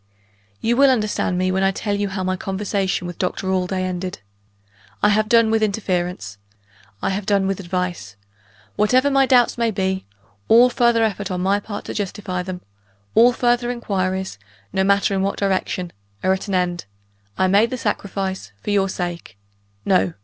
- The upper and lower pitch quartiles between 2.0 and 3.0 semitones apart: Yes, narrow, 2.6 semitones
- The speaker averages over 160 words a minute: Yes, average, 175 wpm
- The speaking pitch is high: Yes, high, 195 Hz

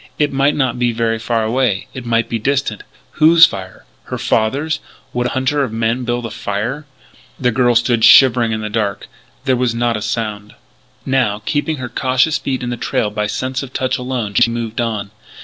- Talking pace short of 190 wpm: No, average, 200 wpm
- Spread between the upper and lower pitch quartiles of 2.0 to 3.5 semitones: Yes, average, 2.7 semitones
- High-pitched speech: No, low, 120 Hz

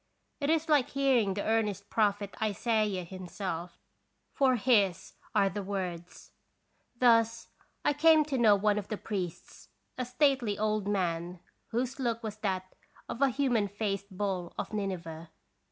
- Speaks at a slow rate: No, average, 145 wpm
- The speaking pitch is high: Yes, high, 210 Hz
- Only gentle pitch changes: No, average, 4.0 semitones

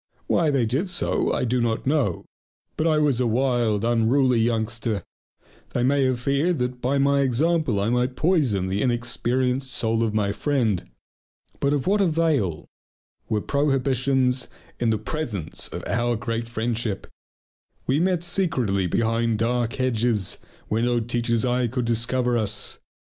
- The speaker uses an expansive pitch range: No, average, 3.4 semitones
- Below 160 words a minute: Yes, average, 150 wpm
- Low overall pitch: Yes, low, 120 Hz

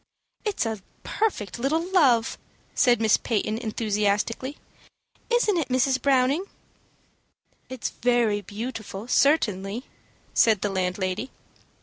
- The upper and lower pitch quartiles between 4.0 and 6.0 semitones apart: Yes, average, 4.4 semitones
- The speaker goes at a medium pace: No, slow, 105 wpm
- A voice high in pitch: Yes, high, 235 Hz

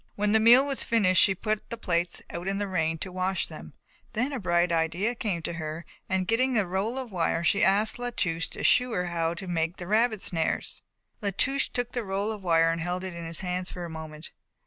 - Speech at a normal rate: No, fast, 235 wpm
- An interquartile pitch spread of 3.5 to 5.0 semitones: Yes, average, 4.4 semitones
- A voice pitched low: No, medium, 185 Hz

